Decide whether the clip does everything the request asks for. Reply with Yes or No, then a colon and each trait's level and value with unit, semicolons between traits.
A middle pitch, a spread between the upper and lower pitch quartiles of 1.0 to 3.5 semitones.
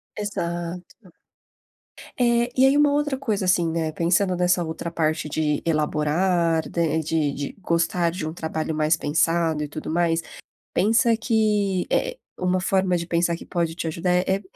Yes: medium, 170 Hz; average, 3.1 semitones